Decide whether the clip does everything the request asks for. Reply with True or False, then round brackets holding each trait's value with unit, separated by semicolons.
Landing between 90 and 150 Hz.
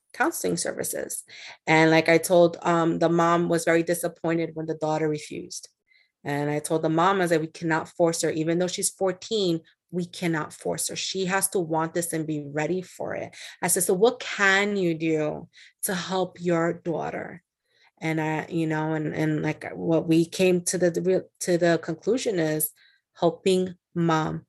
False (165 Hz)